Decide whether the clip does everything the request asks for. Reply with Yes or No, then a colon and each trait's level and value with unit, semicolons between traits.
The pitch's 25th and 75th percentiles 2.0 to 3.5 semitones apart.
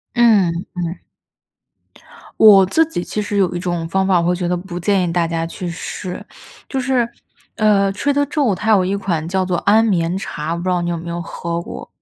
Yes: average, 3.2 semitones